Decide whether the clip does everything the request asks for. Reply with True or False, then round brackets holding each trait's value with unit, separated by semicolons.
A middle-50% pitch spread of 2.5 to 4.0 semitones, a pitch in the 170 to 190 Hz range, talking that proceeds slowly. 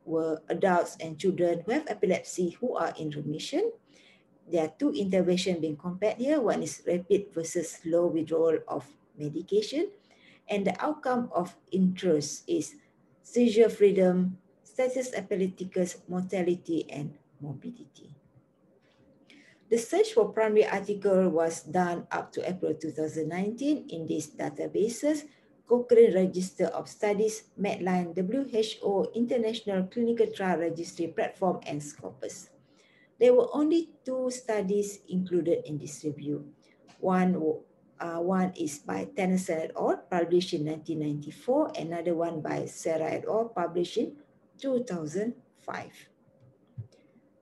False (5.3 semitones; 185 Hz; 120 wpm)